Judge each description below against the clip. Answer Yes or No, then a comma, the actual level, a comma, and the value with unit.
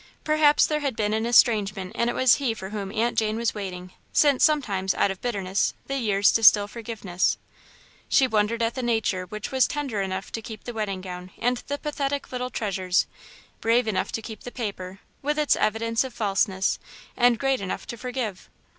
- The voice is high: Yes, high, 225 Hz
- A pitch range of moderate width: Yes, average, 4.0 semitones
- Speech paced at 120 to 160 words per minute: No, average, 190 wpm